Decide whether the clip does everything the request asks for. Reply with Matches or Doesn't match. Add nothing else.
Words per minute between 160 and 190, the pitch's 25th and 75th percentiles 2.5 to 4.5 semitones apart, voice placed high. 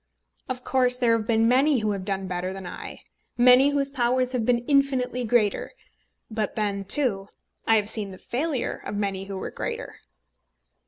Matches